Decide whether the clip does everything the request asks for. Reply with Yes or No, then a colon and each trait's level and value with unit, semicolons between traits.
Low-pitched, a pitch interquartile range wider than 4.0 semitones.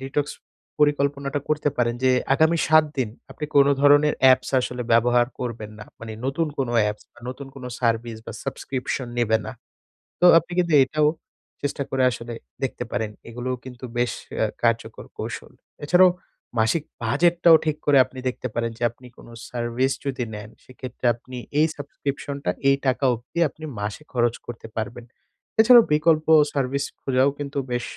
No: low, 130 Hz; average, 3.4 semitones